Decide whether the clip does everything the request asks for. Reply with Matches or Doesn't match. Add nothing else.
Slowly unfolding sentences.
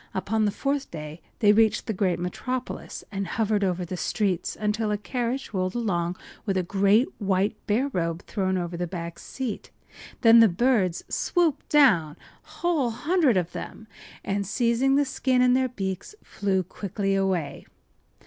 Doesn't match